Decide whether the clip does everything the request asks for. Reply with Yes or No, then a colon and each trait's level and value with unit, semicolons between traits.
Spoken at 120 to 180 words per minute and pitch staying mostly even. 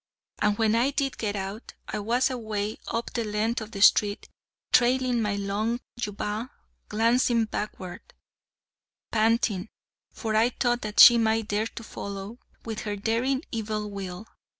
Yes: average, 150 wpm; narrow, 2.1 semitones